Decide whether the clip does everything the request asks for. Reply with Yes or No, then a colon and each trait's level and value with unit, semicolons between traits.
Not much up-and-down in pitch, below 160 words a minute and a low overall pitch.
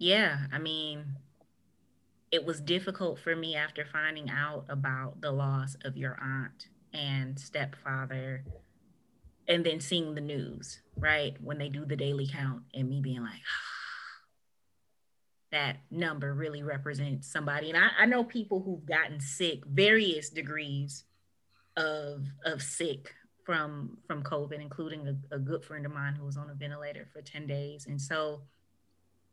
No: narrow, 2.3 semitones; average, 150 wpm; medium, 145 Hz